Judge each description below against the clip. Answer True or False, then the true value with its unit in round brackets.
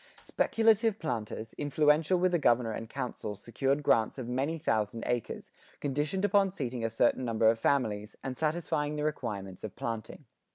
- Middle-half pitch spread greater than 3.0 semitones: True (5.3 semitones)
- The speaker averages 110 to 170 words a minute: True (160 wpm)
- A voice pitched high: False (130 Hz)